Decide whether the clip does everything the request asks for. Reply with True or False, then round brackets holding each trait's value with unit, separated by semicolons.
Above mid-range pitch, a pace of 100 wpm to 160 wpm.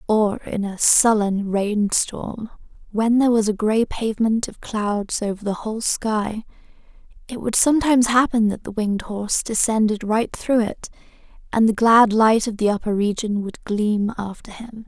False (215 Hz; 170 wpm)